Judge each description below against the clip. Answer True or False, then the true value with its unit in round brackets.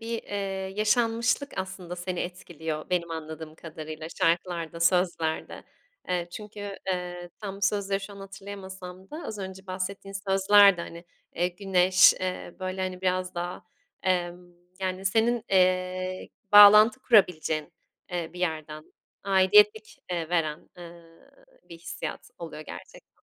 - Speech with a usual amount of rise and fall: False (2.3 semitones)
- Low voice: False (185 Hz)